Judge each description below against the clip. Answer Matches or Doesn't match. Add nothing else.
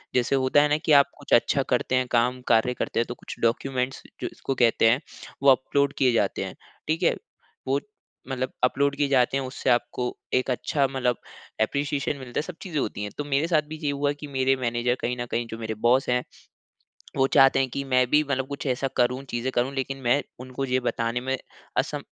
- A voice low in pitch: Matches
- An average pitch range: Doesn't match